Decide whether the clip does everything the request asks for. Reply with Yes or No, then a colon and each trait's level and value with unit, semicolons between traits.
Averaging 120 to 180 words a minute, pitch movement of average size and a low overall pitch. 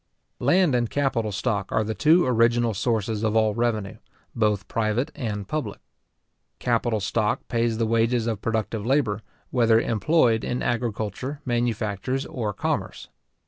No: average, 140 wpm; narrow, 2.3 semitones; low, 115 Hz